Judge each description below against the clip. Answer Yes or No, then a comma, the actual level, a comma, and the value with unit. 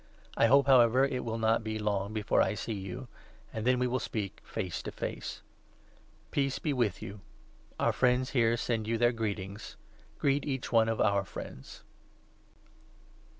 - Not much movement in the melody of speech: No, average, 3.1 semitones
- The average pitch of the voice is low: Yes, low, 115 Hz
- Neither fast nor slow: Yes, average, 170 wpm